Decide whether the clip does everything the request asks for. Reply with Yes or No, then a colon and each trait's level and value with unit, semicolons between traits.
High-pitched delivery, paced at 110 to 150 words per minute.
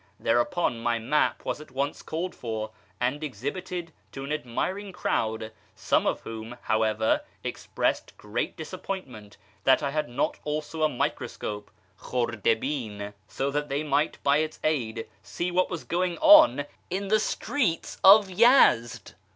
No: medium, 145 Hz; average, 145 wpm